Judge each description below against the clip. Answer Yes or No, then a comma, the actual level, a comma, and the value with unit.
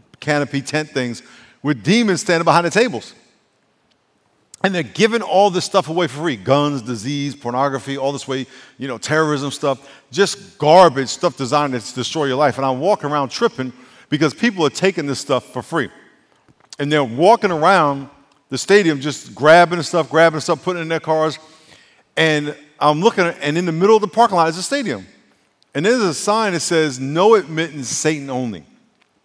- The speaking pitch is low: No, medium, 155 Hz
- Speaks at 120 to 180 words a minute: No, average, 190 wpm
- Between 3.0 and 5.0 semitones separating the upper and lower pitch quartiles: Yes, average, 4.3 semitones